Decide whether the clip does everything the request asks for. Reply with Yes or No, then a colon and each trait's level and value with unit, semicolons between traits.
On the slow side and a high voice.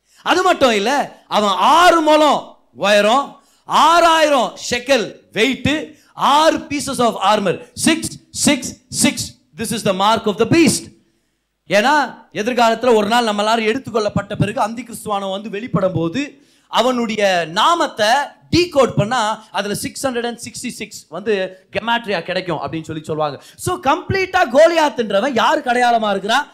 Yes: slow, 40 wpm; high, 230 Hz